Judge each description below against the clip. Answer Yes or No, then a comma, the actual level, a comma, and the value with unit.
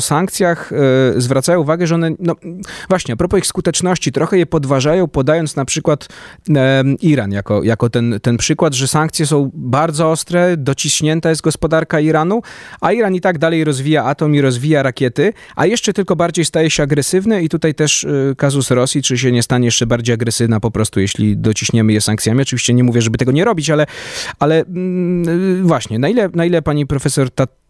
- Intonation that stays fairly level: No, average, 4.5 semitones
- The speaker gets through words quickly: Yes, fast, 190 wpm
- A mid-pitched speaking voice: Yes, medium, 150 Hz